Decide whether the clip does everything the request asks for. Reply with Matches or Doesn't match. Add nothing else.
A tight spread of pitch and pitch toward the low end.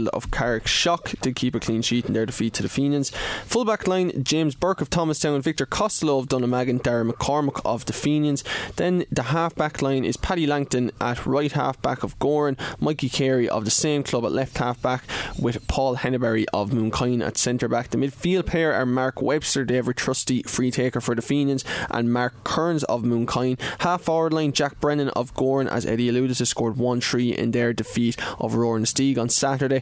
Doesn't match